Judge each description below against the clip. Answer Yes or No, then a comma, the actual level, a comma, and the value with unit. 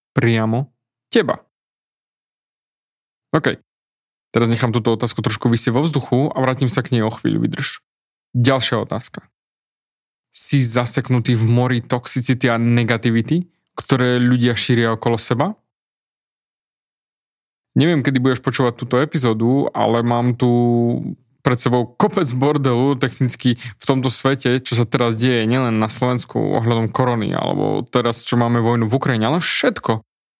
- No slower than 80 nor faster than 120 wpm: No, average, 135 wpm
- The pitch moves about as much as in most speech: No, narrow, 2.0 semitones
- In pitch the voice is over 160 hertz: No, low, 125 Hz